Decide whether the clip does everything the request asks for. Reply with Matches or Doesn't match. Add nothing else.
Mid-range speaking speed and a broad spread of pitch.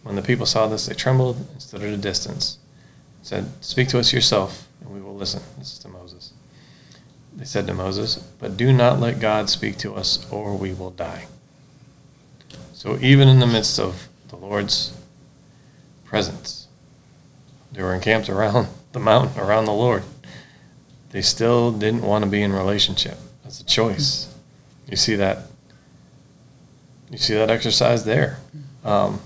Doesn't match